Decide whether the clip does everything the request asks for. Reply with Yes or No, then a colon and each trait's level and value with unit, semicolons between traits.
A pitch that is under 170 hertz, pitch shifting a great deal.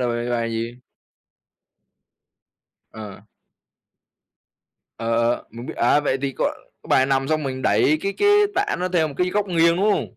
Yes: low, 135 Hz; wide, 6.6 semitones